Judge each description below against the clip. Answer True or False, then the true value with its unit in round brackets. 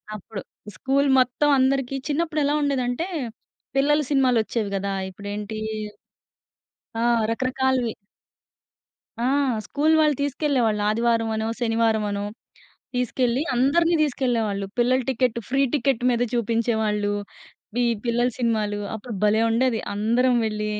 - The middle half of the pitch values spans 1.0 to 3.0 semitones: False (3.5 semitones)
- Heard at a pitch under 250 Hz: True (240 Hz)